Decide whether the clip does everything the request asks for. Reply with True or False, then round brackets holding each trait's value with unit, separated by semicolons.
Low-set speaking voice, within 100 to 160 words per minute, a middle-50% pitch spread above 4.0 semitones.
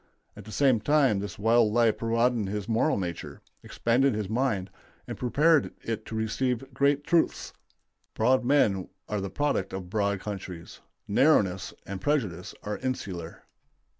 True (110 Hz; 145 wpm; 4.9 semitones)